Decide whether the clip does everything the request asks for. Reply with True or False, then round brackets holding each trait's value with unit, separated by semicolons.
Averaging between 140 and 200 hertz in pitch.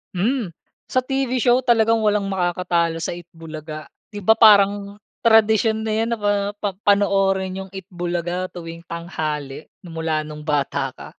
True (190 Hz)